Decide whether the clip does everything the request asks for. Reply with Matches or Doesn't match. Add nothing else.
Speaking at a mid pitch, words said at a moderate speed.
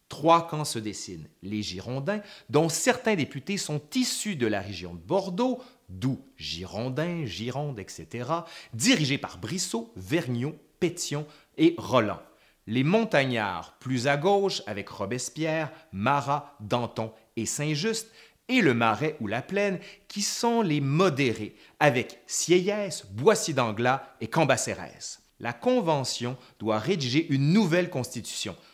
Doesn't match